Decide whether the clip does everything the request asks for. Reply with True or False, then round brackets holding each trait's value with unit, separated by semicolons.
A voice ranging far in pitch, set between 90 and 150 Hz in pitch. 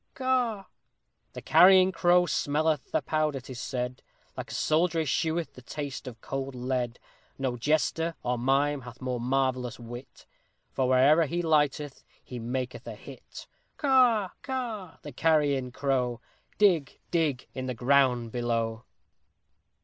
False (4.6 semitones; 135 Hz)